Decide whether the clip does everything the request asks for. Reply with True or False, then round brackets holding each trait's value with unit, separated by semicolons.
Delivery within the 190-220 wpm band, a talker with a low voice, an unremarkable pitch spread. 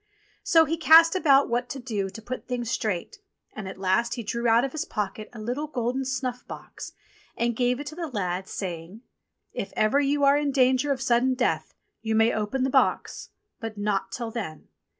False (200 wpm; 240 Hz; 4.0 semitones)